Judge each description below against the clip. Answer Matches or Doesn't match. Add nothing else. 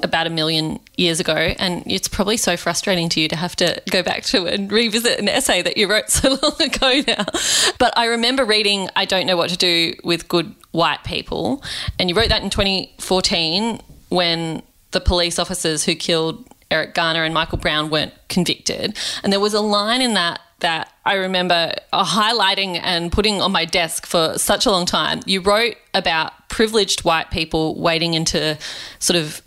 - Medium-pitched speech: Matches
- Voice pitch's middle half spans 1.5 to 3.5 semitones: Doesn't match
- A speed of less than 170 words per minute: Doesn't match